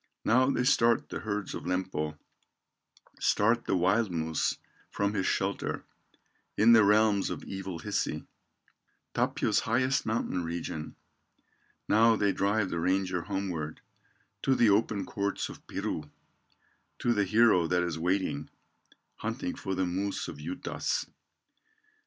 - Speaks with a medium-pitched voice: No, low, 100 Hz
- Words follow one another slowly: Yes, slow, 130 wpm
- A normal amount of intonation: Yes, average, 3.7 semitones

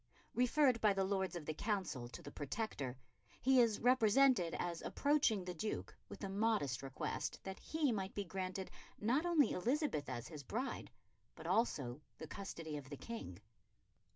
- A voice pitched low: No, high, 195 Hz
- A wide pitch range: Yes, wide, 7.2 semitones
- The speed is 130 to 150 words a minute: No, average, 165 wpm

